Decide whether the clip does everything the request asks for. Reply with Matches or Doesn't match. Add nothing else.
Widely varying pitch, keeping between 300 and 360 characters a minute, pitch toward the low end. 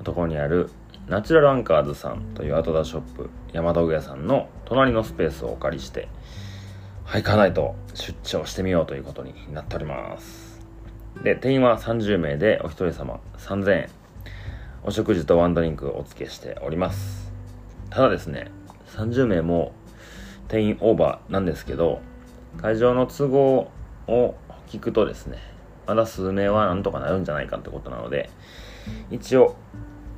Doesn't match